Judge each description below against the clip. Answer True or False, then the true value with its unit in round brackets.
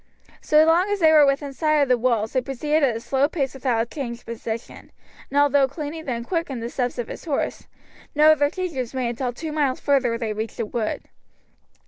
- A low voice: False (270 Hz)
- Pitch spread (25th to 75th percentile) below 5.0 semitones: True (4.1 semitones)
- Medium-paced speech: False (215 wpm)